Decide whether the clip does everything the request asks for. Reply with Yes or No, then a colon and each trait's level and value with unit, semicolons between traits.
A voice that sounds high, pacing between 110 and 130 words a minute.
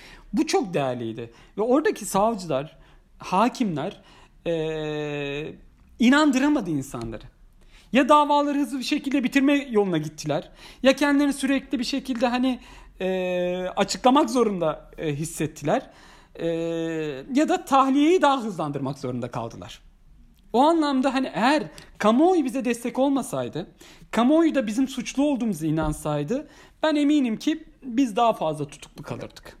Yes: high, 220 Hz; average, 120 wpm